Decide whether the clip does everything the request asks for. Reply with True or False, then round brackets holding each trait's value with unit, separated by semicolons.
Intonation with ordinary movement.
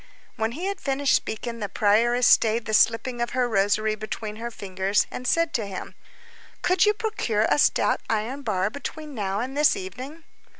True (4.3 semitones)